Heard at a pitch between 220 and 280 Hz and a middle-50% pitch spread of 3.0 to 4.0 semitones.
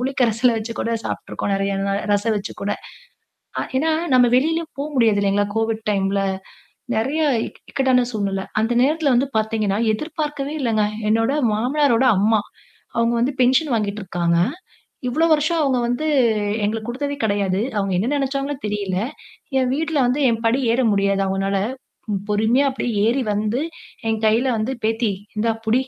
No: high, 225 Hz; average, 4.4 semitones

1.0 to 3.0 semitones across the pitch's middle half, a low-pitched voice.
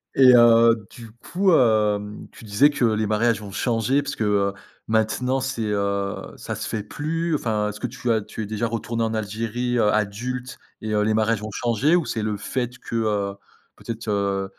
Yes: narrow, 2.6 semitones; low, 110 Hz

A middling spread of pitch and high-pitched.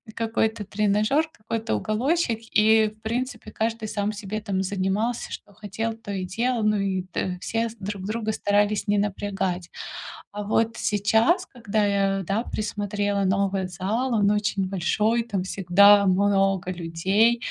No: narrow, 2.3 semitones; high, 205 Hz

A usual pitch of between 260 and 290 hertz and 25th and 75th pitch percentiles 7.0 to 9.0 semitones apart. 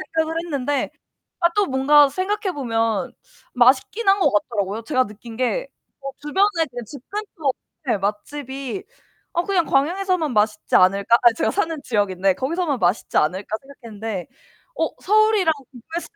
Yes: very high, 270 Hz; wide, 7.4 semitones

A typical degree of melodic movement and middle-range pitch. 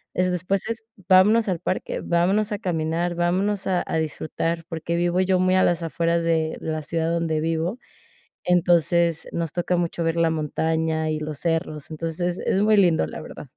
No: narrow, 2.1 semitones; medium, 170 Hz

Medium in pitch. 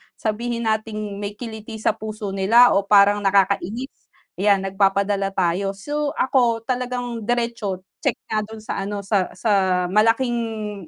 No: high, 215 Hz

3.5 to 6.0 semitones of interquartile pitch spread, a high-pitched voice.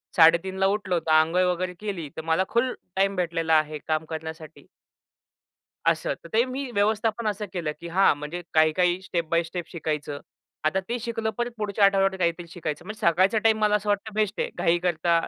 No: average, 4.2 semitones; medium, 180 Hz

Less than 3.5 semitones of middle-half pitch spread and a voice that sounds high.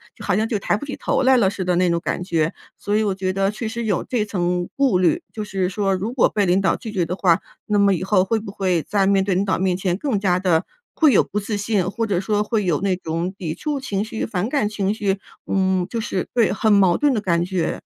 Yes: average, 2.8 semitones; high, 195 Hz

